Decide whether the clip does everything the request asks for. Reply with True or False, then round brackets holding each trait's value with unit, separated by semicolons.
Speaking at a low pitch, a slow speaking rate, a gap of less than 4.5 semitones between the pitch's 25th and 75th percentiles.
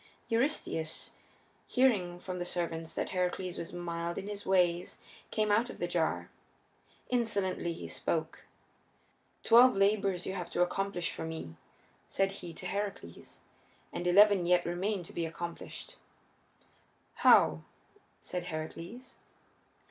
False (180 Hz; 125 wpm; 2.8 semitones)